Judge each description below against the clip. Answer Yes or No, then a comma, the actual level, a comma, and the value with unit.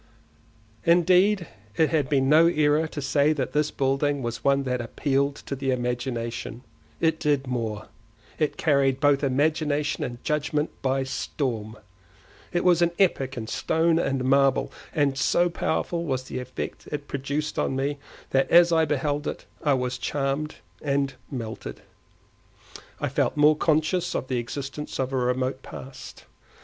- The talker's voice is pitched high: No, medium, 140 Hz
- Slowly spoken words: No, average, 150 wpm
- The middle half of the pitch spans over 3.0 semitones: No, average, 2.7 semitones